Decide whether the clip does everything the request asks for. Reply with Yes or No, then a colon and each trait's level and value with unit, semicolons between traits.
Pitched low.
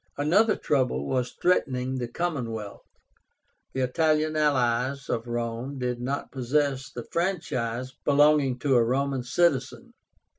Yes: low, 130 Hz